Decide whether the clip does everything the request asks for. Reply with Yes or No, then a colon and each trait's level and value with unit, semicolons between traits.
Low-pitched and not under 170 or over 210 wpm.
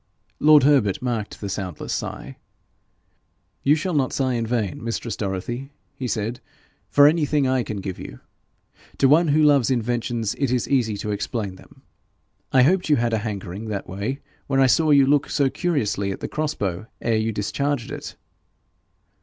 Yes: low, 120 Hz; average, 175 wpm